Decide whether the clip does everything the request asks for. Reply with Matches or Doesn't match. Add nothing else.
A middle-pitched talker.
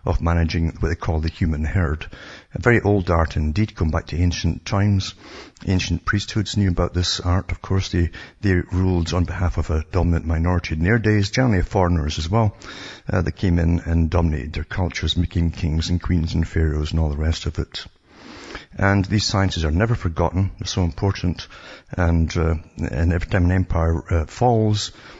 Doesn't match